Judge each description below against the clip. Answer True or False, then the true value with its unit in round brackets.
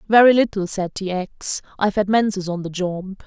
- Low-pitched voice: False (195 Hz)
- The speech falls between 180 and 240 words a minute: True (200 wpm)